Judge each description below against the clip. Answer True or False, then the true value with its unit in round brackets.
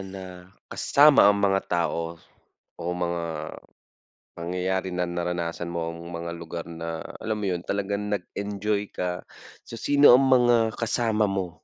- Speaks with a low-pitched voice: True (90 Hz)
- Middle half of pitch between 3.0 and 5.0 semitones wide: True (3.3 semitones)